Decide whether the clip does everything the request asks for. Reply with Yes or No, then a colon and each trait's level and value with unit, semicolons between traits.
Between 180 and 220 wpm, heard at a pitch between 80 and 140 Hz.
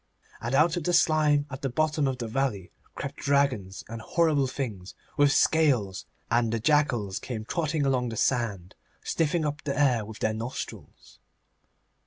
No: average, 165 wpm; low, 135 Hz